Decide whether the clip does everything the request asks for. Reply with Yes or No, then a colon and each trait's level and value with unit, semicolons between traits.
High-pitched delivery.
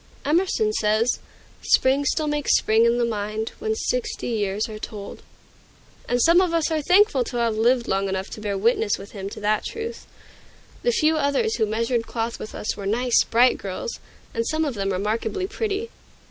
Yes: high, 235 Hz